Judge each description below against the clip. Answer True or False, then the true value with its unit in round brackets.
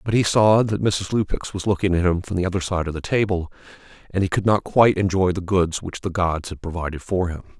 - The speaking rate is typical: False (255 wpm)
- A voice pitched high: False (95 Hz)